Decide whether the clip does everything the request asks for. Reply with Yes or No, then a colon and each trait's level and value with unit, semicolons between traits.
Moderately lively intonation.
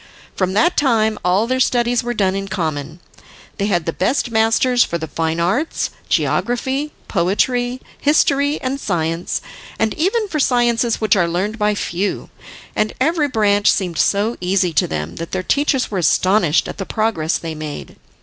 No: wide, 5.8 semitones